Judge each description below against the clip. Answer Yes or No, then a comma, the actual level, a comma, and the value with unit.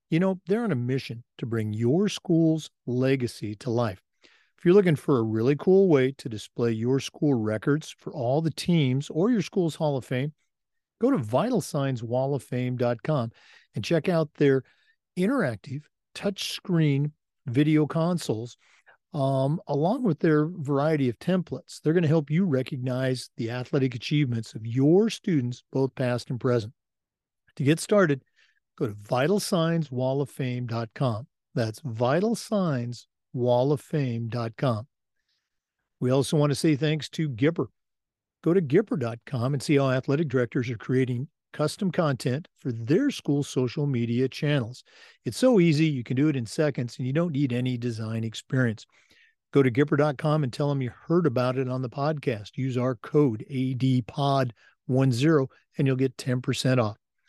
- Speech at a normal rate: Yes, average, 150 wpm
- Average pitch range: Yes, average, 3.8 semitones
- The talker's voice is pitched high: No, low, 135 Hz